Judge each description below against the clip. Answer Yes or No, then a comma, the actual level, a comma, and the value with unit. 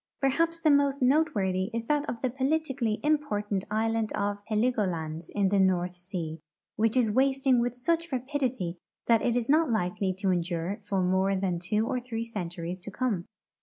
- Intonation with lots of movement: Yes, wide, 5.8 semitones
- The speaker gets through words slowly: No, average, 170 wpm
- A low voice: No, high, 220 Hz